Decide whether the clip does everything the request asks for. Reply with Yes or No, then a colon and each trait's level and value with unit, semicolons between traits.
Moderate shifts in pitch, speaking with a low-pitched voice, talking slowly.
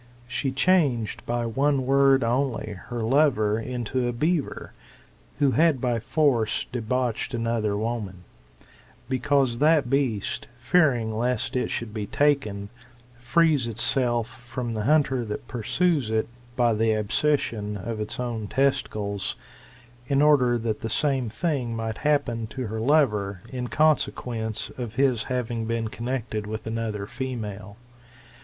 Yes: average, 3.5 semitones; low, 120 Hz; slow, 130 wpm